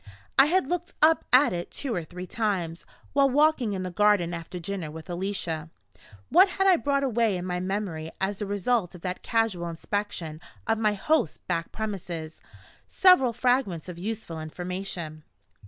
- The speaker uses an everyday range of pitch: No, wide, 6.0 semitones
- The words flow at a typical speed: Yes, average, 170 wpm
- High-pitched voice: Yes, high, 195 Hz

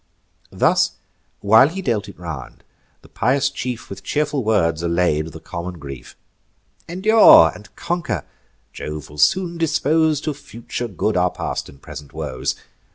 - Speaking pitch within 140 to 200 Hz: No, low, 105 Hz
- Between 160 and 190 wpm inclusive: No, average, 145 wpm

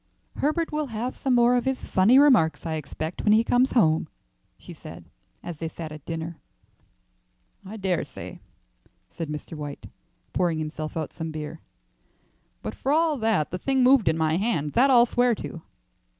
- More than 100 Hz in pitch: Yes, high, 190 Hz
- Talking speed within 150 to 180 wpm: Yes, average, 175 wpm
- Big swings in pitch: Yes, wide, 7.7 semitones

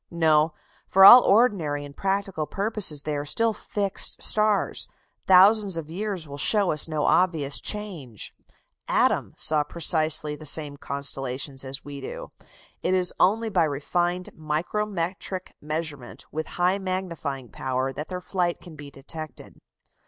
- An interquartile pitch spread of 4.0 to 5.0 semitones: Yes, average, 4.7 semitones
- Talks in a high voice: No, medium, 165 Hz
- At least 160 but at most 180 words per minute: No, average, 140 wpm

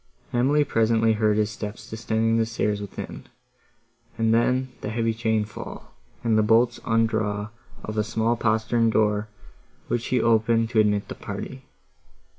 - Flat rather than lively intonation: Yes, narrow, 1.3 semitones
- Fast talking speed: No, average, 150 wpm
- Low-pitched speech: Yes, low, 110 Hz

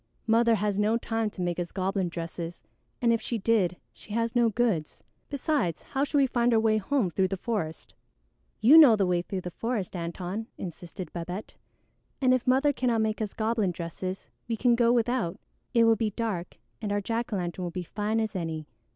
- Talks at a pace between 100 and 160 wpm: No, fast, 205 wpm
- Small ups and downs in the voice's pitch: No, average, 4.5 semitones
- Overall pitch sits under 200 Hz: No, high, 215 Hz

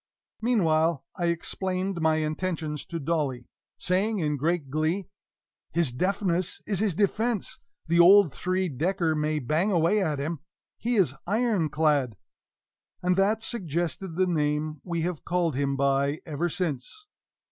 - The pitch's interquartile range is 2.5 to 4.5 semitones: Yes, average, 3.7 semitones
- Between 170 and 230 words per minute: No, average, 140 wpm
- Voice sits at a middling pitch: Yes, medium, 170 Hz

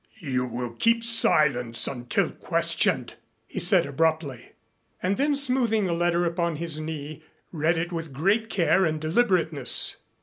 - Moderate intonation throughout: Yes, average, 4.9 semitones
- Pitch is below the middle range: No, medium, 165 Hz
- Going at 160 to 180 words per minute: No, average, 145 wpm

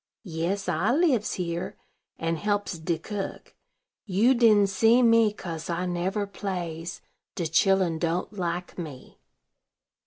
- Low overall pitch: No, medium, 185 Hz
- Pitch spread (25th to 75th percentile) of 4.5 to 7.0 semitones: No, average, 3.6 semitones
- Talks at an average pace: No, slow, 125 wpm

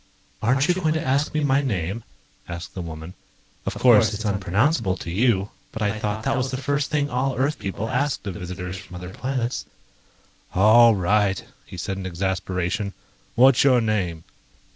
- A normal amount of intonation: No, wide, 5.8 semitones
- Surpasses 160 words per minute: Yes, average, 175 wpm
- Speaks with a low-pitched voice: Yes, low, 110 Hz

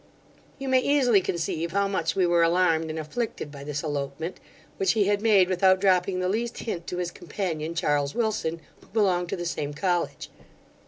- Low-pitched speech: No, medium, 180 Hz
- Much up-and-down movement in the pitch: No, average, 3.6 semitones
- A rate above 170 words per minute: Yes, average, 190 wpm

